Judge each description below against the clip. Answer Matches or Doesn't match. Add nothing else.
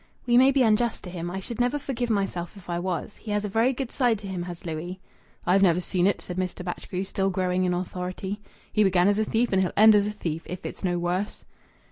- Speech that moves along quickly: Matches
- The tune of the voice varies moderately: Matches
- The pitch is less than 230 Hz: Matches